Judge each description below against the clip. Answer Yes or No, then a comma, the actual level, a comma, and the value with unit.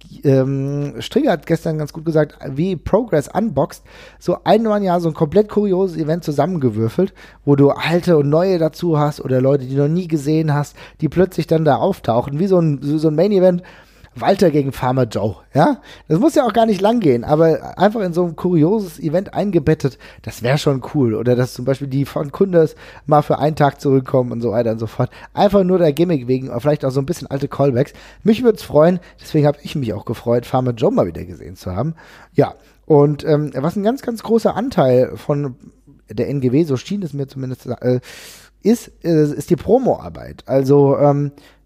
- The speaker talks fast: Yes, fast, 205 wpm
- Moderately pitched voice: Yes, medium, 150 Hz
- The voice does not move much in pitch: No, average, 4.5 semitones